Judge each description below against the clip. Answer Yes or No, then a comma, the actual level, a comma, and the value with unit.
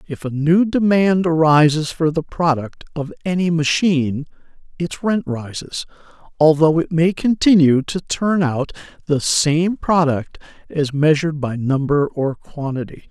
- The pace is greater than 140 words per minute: No, slow, 135 wpm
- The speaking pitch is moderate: Yes, medium, 160 Hz